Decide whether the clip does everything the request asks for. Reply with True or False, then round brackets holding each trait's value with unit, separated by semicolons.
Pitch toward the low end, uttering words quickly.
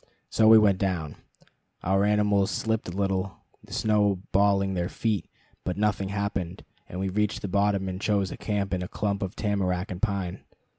False (100 Hz; 185 wpm)